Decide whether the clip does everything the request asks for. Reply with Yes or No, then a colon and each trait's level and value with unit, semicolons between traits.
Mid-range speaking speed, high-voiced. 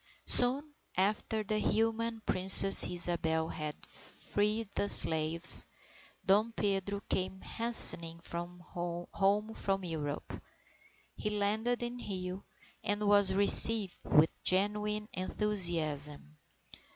No: slow, 100 wpm; high, 195 Hz